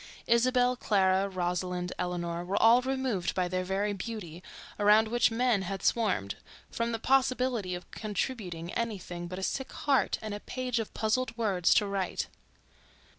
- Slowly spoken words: No, average, 155 wpm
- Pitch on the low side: No, high, 205 Hz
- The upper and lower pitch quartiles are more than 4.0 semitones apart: Yes, average, 4.5 semitones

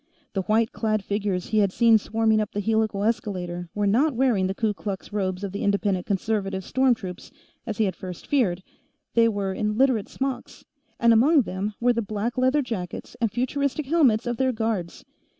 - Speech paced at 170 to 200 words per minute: Yes, average, 190 wpm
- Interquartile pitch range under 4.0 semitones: Yes, average, 3.4 semitones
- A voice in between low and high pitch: No, high, 215 Hz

